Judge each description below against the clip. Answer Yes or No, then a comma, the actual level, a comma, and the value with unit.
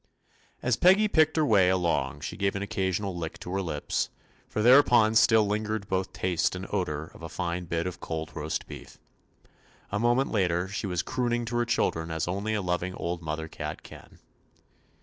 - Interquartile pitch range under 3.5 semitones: No, average, 4.3 semitones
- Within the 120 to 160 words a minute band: No, average, 190 wpm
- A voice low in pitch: Yes, very low, 95 Hz